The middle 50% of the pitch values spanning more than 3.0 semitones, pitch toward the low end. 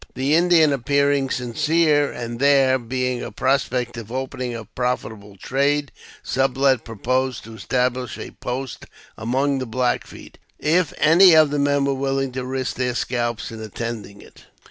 No: average, 2.7 semitones; low, 130 Hz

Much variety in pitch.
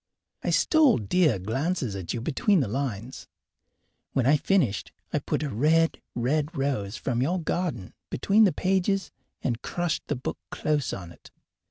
Yes: wide, 6.9 semitones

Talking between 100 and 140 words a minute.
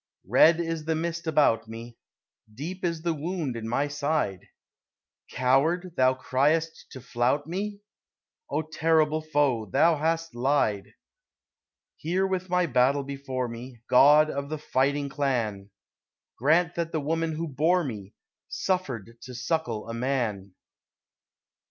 Yes: slow, 135 wpm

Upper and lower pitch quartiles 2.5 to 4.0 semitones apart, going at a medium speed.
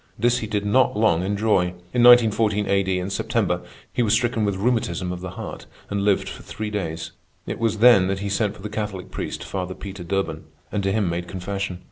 No: average, 2.8 semitones; fast, 210 wpm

